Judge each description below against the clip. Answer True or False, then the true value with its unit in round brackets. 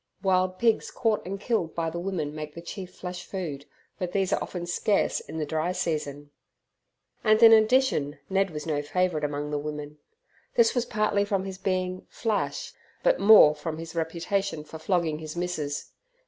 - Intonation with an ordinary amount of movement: True (4.4 semitones)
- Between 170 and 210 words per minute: True (175 wpm)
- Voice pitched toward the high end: False (180 Hz)